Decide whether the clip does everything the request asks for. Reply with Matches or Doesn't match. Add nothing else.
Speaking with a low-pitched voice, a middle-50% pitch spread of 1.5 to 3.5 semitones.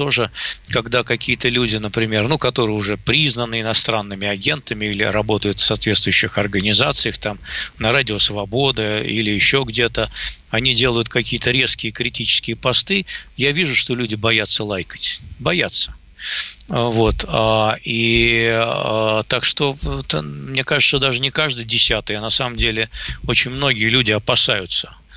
Matches